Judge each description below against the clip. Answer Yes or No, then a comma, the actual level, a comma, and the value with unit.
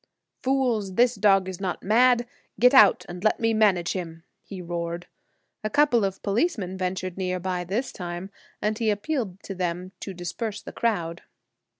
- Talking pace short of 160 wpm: No, average, 170 wpm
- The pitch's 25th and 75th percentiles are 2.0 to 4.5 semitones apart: Yes, average, 3.9 semitones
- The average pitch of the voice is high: Yes, high, 195 Hz